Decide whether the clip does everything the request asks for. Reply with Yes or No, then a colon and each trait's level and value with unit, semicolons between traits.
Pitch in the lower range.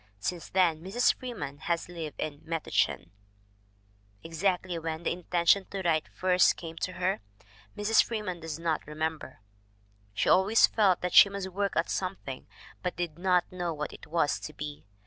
No: medium, 175 Hz